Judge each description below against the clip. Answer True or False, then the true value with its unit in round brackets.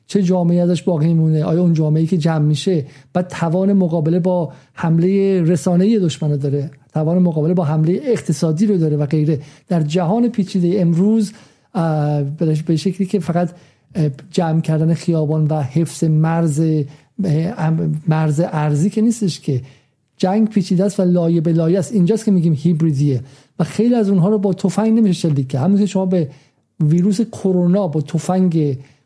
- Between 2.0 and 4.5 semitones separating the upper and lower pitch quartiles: True (3.3 semitones)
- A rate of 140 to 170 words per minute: True (155 wpm)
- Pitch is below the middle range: False (170 Hz)